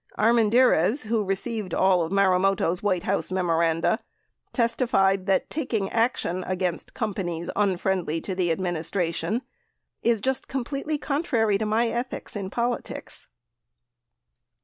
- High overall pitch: Yes, high, 195 Hz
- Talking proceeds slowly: Yes, slow, 115 wpm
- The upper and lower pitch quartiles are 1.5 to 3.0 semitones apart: No, average, 4.3 semitones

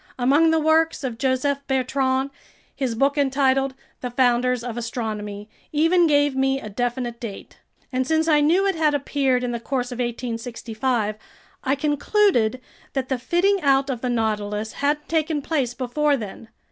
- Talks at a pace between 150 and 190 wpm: Yes, average, 160 wpm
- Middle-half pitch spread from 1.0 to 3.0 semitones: No, average, 3.4 semitones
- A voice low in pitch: No, very high, 265 Hz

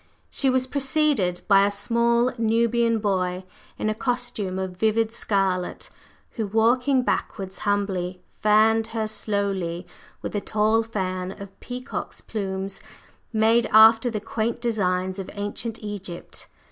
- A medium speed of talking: No, slow, 130 wpm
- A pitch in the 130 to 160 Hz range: No, high, 215 Hz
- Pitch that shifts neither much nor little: Yes, average, 3.1 semitones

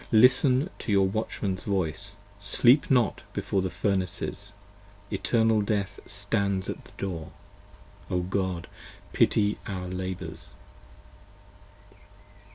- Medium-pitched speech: No, low, 100 Hz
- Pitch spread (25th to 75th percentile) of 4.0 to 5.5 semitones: No, average, 2.7 semitones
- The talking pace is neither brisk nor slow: No, slow, 105 wpm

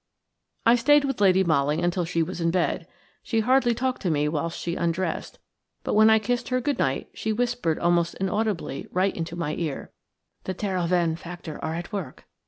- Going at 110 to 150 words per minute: No, average, 190 wpm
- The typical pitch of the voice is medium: Yes, medium, 180 Hz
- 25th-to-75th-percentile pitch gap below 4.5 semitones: No, average, 4.8 semitones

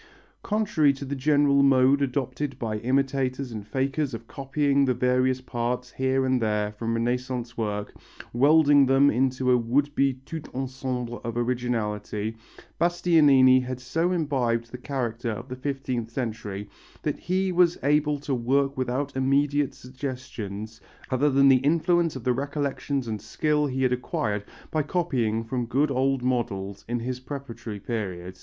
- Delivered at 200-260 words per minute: No, average, 150 wpm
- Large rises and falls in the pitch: No, average, 3.0 semitones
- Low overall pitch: Yes, low, 130 Hz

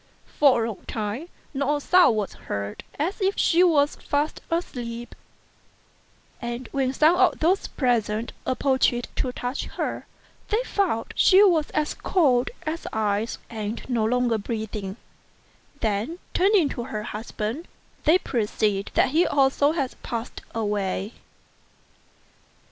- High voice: Yes, very high, 250 Hz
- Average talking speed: No, slow, 130 wpm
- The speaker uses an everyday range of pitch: No, wide, 5.9 semitones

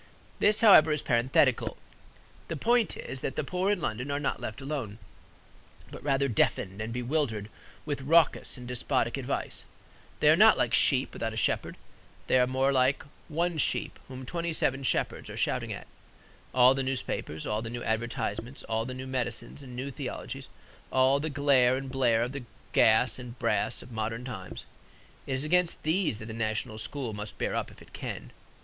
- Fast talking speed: No, average, 185 wpm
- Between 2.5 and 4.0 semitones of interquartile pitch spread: Yes, average, 3.6 semitones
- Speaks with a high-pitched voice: No, low, 130 Hz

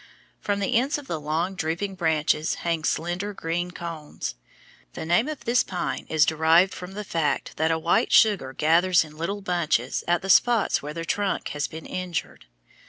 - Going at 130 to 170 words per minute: No, average, 180 wpm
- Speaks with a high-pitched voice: No, medium, 170 Hz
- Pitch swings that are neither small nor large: Yes, average, 3.3 semitones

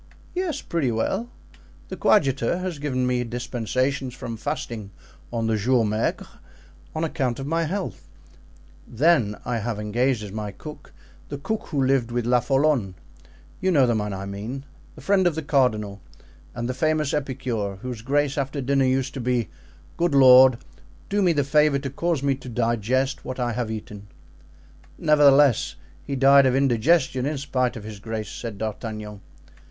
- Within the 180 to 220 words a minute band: No, average, 160 wpm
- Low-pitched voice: Yes, low, 130 Hz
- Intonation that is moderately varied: Yes, average, 4.0 semitones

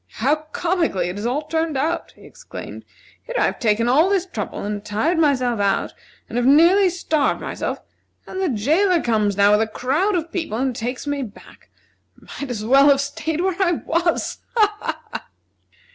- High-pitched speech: Yes, very high, 285 Hz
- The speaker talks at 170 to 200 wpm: Yes, average, 185 wpm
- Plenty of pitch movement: Yes, wide, 6.8 semitones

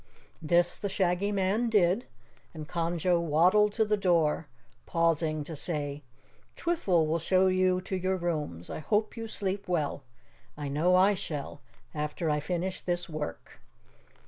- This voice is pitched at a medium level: Yes, medium, 175 Hz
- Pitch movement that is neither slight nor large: Yes, average, 3.5 semitones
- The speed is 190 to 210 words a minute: No, average, 145 wpm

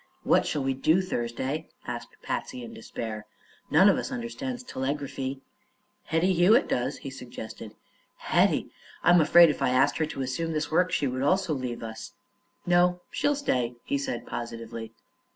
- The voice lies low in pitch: No, medium, 150 Hz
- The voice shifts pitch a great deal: Yes, wide, 6.5 semitones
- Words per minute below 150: No, average, 160 wpm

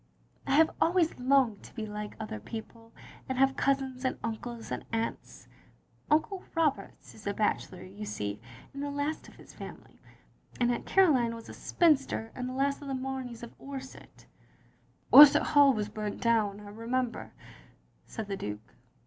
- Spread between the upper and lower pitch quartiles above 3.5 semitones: Yes, average, 4.3 semitones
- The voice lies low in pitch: No, high, 245 Hz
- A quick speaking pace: No, average, 170 wpm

